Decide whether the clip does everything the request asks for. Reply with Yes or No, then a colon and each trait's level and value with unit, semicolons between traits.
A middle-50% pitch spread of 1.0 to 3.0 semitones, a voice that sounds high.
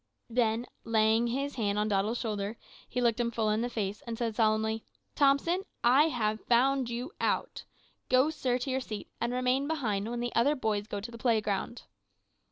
Yes: average, 2.7 semitones; high, 235 Hz